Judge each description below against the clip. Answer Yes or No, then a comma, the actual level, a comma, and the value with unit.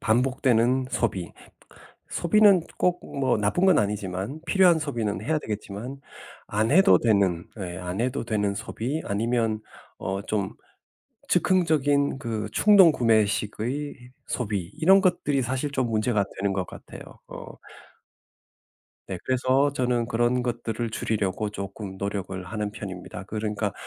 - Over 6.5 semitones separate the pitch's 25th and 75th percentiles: No, average, 5.2 semitones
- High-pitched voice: No, low, 115 Hz